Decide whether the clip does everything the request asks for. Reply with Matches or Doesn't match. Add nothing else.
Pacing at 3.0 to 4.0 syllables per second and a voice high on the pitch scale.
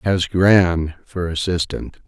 Doesn't match